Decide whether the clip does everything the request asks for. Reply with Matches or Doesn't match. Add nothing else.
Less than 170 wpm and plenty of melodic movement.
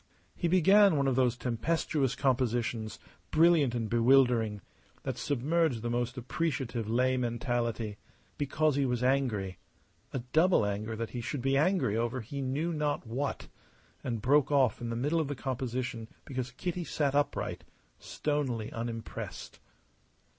Doesn't match